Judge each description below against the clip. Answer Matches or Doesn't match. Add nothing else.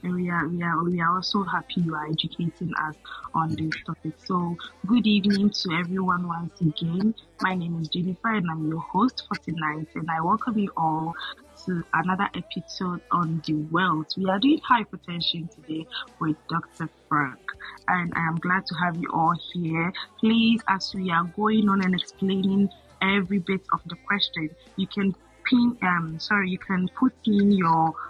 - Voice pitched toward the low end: Doesn't match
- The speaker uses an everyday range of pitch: Matches